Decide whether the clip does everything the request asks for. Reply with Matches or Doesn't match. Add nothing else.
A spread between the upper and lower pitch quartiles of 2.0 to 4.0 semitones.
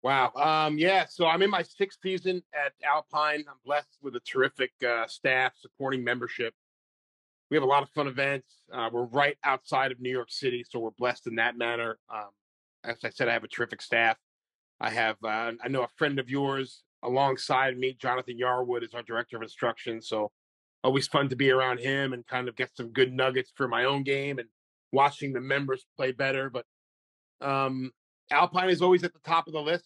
Matches